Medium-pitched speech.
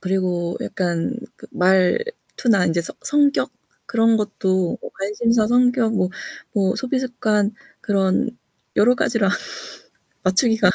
No: high, 210 Hz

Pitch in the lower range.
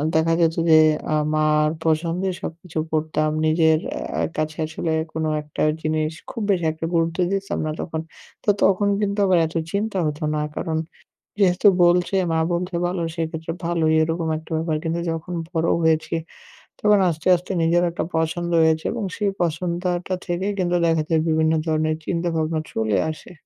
No: medium, 165 Hz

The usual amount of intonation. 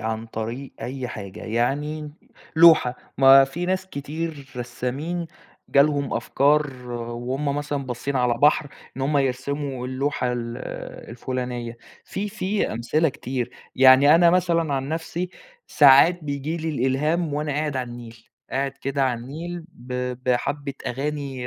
Yes: average, 3.4 semitones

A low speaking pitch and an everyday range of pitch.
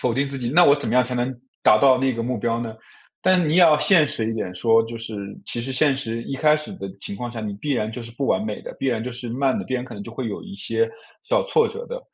Yes: low, 130 Hz; average, 4.7 semitones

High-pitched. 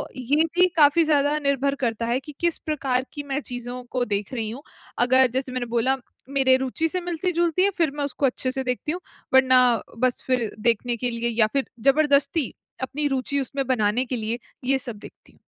Yes: very high, 265 Hz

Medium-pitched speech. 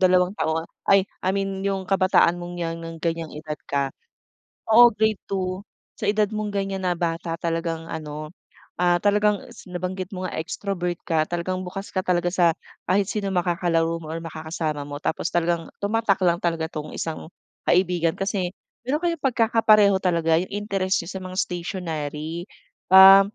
Yes: medium, 180 Hz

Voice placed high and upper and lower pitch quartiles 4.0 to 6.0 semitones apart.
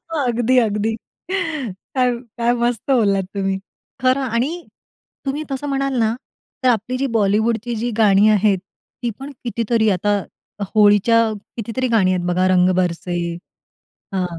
Yes: high, 225 Hz; average, 4.3 semitones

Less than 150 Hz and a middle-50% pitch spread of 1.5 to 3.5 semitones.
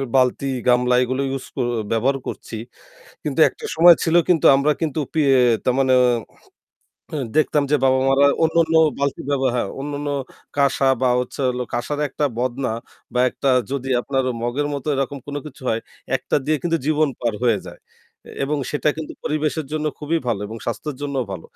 Yes: medium, 140 Hz; average, 2.9 semitones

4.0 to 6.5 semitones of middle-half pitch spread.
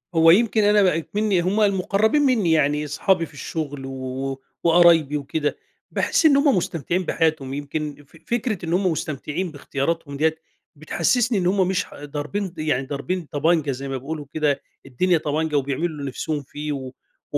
Yes: average, 4.4 semitones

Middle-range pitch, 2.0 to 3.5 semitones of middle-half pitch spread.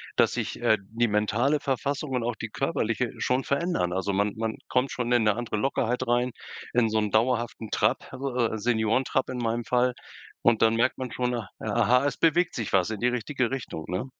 No: low, 120 Hz; average, 2.7 semitones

